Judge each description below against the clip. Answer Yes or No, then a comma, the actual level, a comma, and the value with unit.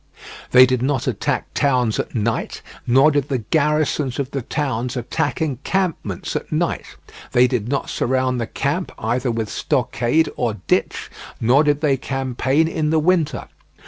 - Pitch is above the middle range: No, low, 130 Hz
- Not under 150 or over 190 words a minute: Yes, average, 155 wpm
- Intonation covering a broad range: No, average, 3.4 semitones